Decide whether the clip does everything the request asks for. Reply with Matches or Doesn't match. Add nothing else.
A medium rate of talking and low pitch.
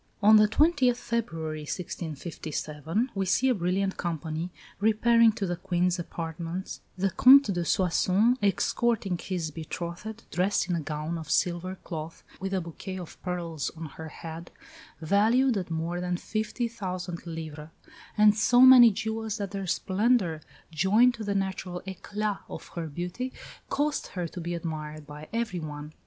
Doesn't match